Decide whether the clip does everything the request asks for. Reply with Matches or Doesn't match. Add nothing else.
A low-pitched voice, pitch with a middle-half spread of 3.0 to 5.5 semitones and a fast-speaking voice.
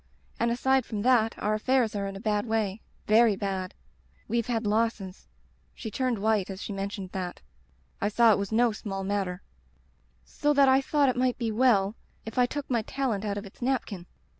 Doesn't match